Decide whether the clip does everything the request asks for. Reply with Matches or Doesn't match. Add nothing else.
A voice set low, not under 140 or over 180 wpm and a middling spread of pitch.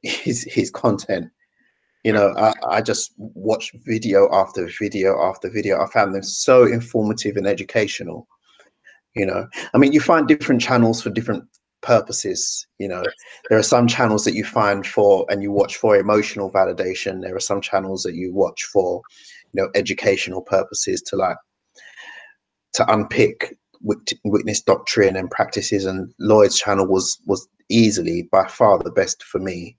Doesn't match